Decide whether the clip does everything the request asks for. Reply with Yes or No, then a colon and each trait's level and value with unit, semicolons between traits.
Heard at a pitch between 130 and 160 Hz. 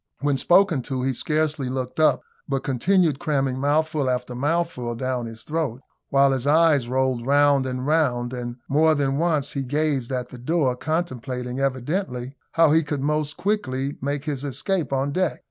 Yes: medium, 140 Hz